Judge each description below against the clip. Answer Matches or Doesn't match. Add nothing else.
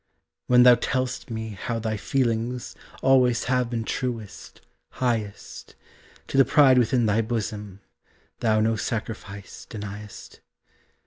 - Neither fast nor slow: Doesn't match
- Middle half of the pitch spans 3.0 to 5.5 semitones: Doesn't match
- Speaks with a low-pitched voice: Matches